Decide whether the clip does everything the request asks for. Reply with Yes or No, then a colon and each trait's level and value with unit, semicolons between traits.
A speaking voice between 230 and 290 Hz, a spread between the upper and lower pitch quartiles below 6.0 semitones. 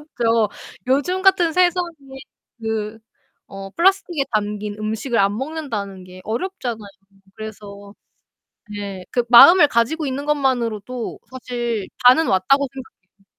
Yes: high, 235 Hz; wide, 5.5 semitones